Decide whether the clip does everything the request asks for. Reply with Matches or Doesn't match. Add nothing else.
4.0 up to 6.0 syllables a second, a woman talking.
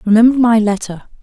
Matches